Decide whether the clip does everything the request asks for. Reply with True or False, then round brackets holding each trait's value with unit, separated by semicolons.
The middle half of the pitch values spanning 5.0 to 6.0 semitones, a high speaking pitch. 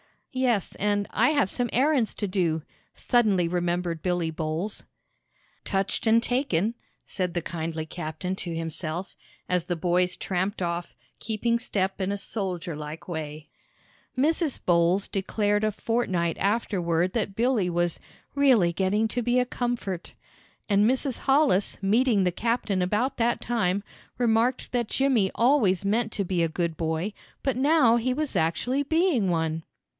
True (5.5 semitones; 200 Hz)